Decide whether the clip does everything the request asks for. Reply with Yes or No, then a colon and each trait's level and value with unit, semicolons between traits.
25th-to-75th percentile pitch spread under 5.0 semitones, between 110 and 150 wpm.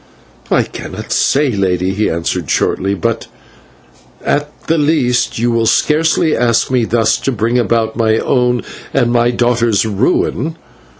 Yes: average, 2.8 semitones; average, 140 wpm